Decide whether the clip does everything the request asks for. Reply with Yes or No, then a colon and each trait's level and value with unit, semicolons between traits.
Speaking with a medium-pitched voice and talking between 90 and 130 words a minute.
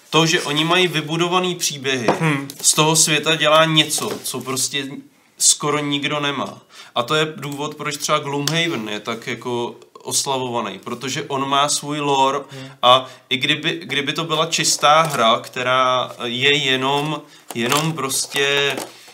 No: medium, 145 Hz; average, 140 wpm